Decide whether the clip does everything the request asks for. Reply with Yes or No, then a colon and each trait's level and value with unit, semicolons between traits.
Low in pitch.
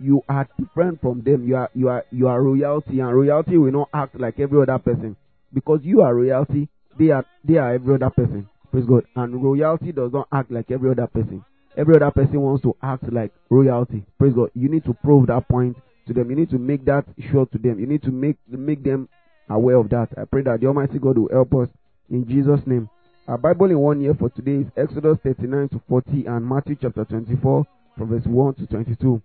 Yes: low, 130 Hz